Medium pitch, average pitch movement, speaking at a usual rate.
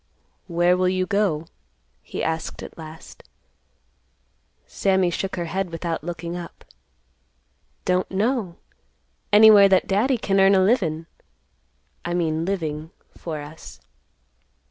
No: medium, 180 Hz; average, 3.0 semitones; slow, 110 wpm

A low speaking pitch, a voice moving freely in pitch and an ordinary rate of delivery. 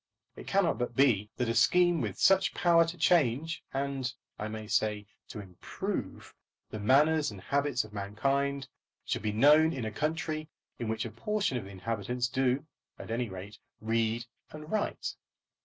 Yes: low, 125 Hz; wide, 6.0 semitones; average, 170 wpm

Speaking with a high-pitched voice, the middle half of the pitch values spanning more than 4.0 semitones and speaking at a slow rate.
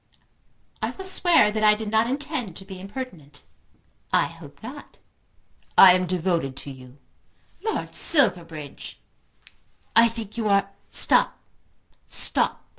Yes: high, 200 Hz; average, 5.2 semitones; slow, 130 wpm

